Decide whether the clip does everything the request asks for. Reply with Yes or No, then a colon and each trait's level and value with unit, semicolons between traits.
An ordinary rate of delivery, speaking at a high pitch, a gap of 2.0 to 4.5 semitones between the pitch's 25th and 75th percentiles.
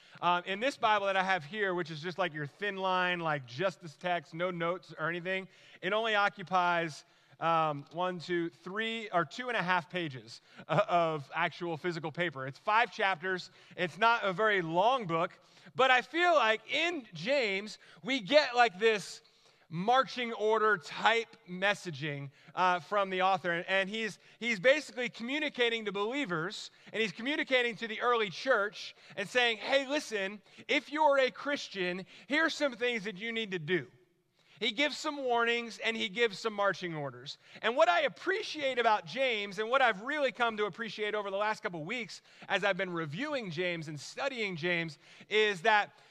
No: average, 175 wpm; high, 200 Hz; average, 4.9 semitones